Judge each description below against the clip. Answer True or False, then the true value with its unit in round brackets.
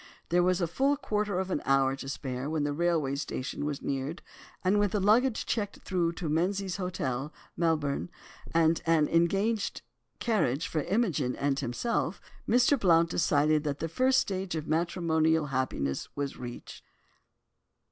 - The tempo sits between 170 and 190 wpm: False (155 wpm)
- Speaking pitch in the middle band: True (165 Hz)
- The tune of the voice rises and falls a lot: False (5.0 semitones)